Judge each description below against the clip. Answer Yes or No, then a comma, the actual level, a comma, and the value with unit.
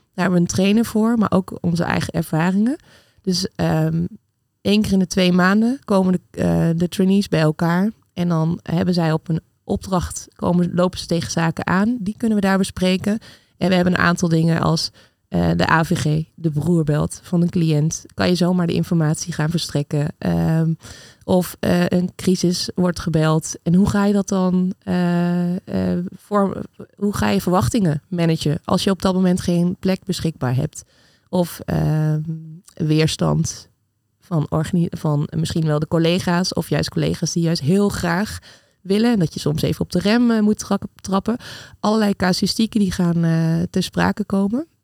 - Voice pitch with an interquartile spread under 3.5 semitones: Yes, average, 3.1 semitones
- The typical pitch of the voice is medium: Yes, medium, 175 Hz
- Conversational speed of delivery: Yes, average, 180 wpm